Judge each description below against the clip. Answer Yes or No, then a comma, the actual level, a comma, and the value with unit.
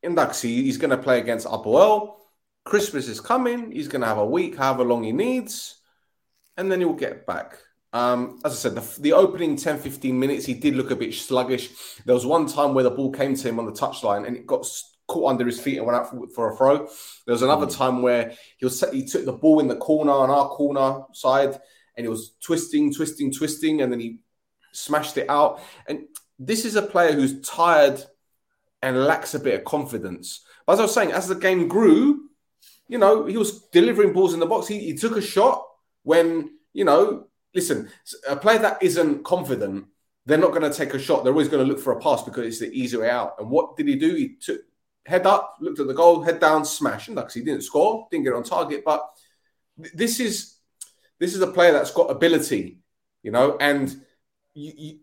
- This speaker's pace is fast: Yes, fast, 225 wpm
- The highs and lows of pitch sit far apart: Yes, wide, 7.9 semitones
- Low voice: No, medium, 155 Hz